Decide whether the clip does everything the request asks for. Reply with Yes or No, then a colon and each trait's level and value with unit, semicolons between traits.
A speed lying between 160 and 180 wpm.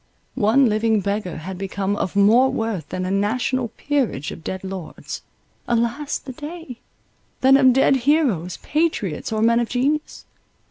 No: average, 145 wpm